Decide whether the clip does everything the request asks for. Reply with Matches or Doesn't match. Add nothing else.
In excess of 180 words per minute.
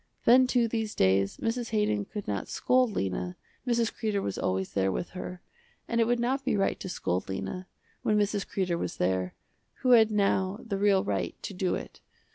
Matches